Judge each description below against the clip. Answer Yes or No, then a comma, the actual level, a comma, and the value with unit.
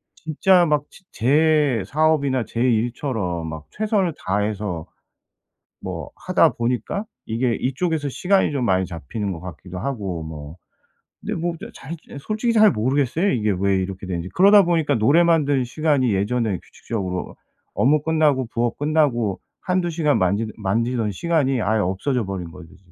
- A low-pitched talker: Yes, low, 125 Hz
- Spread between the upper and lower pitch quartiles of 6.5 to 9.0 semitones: Yes, wide, 7.9 semitones